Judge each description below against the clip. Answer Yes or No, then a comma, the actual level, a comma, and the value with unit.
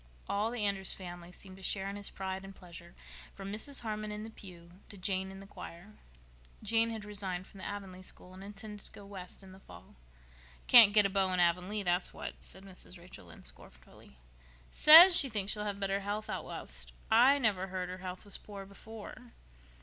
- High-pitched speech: Yes, high, 195 Hz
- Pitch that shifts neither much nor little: No, narrow, 2.2 semitones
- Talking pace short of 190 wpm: No, fast, 205 wpm